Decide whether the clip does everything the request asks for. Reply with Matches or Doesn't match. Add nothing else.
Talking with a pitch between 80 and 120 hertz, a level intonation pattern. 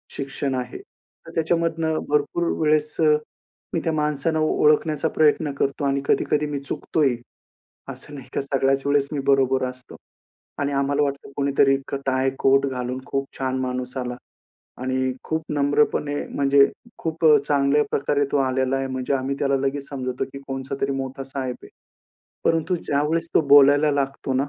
Doesn't match